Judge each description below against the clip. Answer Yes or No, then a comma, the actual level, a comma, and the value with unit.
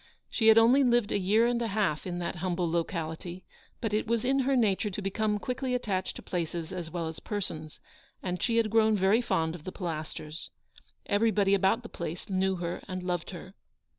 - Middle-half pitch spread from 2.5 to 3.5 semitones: No, average, 4.3 semitones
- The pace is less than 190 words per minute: No, average, 200 wpm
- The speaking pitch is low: No, high, 190 Hz